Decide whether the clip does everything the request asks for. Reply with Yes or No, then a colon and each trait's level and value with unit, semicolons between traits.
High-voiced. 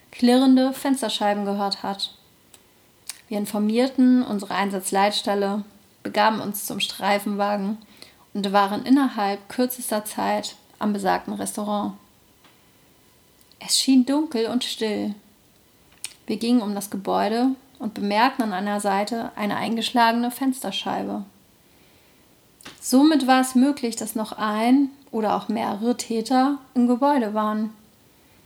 Yes: high, 220 Hz